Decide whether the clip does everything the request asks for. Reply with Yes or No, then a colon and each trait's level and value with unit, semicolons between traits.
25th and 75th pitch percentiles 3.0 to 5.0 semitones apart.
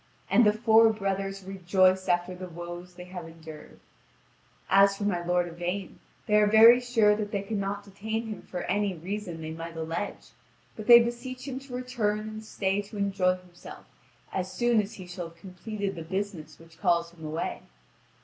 Yes: average, 3.3 semitones